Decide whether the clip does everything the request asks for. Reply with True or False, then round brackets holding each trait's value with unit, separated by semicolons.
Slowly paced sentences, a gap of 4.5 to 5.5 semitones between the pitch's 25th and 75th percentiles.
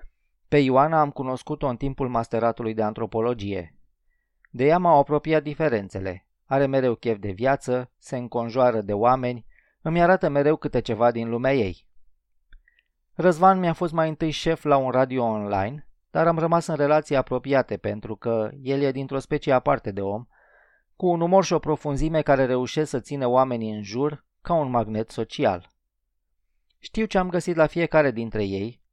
False (170 wpm; 5.1 semitones)